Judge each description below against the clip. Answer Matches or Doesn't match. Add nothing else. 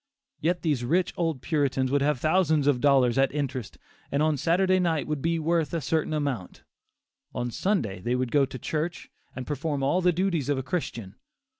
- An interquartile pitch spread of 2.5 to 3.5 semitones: Doesn't match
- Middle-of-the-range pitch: Matches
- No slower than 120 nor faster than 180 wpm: Doesn't match